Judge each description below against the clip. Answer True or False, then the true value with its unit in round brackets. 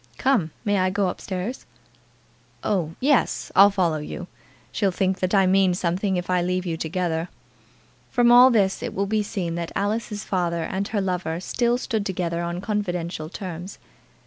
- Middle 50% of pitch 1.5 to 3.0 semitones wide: True (2.7 semitones)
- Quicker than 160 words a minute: True (175 wpm)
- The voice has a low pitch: False (185 Hz)